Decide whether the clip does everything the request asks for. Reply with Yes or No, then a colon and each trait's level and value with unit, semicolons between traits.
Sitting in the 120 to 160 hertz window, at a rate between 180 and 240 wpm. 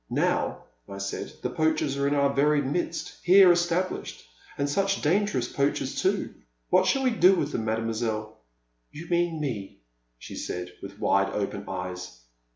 No: medium, 140 Hz; average, 170 wpm